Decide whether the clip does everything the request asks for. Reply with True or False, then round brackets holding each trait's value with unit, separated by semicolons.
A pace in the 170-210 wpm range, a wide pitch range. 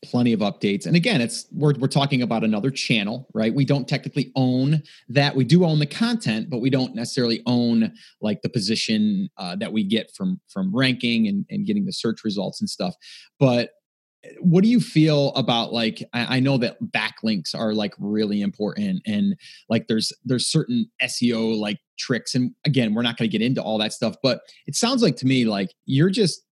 True (205 wpm; 8.0 semitones)